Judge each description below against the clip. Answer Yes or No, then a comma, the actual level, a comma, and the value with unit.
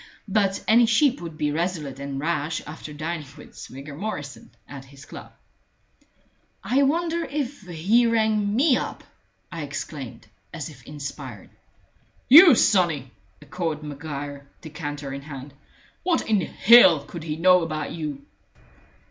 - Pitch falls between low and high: Yes, medium, 160 Hz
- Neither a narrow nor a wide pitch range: No, wide, 6.7 semitones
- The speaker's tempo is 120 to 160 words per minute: Yes, slow, 135 wpm